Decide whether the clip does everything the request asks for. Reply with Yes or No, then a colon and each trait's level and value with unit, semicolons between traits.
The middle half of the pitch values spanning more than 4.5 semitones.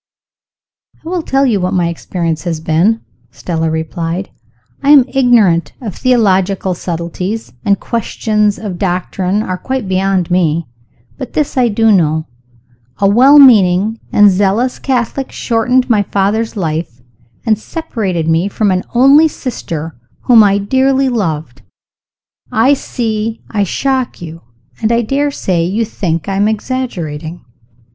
Yes: wide, 5.4 semitones